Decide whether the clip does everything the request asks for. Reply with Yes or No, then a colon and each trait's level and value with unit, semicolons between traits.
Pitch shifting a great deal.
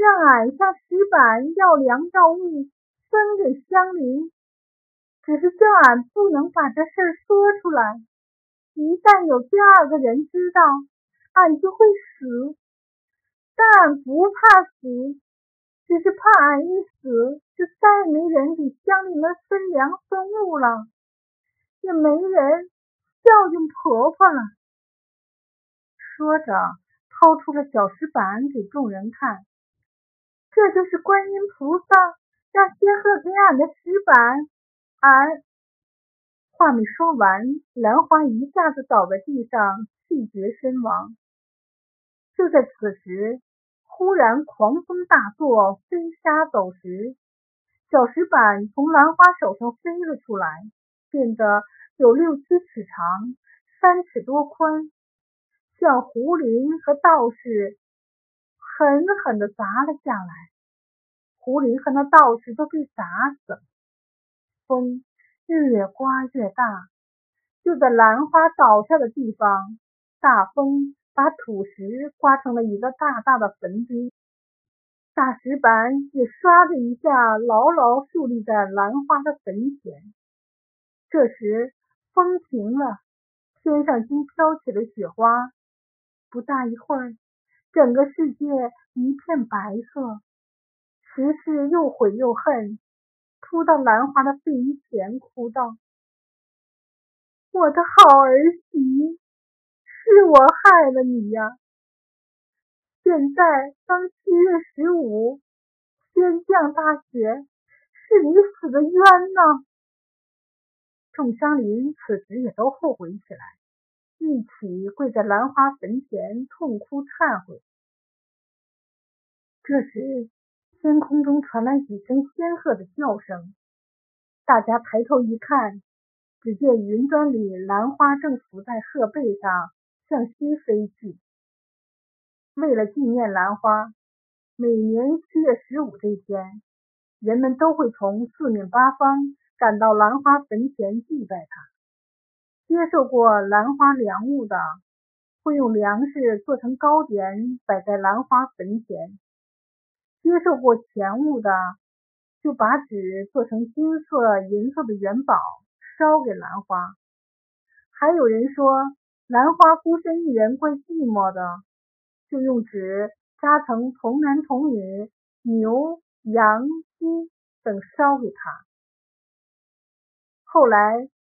Yes: wide, 6.1 semitones